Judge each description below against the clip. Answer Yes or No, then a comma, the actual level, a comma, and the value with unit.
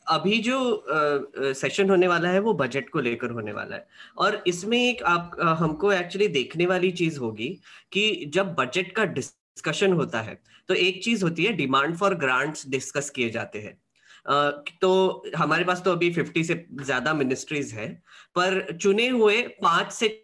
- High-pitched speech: No, medium, 175 Hz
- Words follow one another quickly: No, average, 180 wpm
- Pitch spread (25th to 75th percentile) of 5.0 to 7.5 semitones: Yes, wide, 5.4 semitones